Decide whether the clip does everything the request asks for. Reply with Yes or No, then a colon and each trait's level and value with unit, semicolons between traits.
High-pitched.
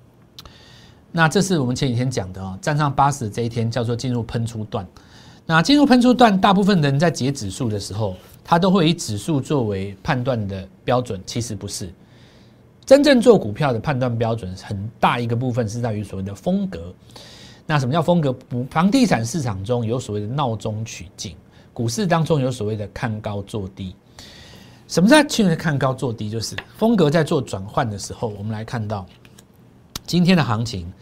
No: low, 120 Hz